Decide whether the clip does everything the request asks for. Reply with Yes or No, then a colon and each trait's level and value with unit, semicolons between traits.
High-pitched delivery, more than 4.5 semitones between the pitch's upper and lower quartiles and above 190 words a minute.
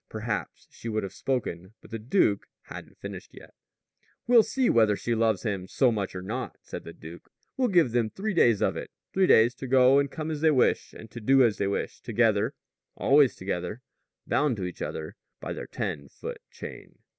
No: low, 115 Hz; average, 5.2 semitones; fast, 205 wpm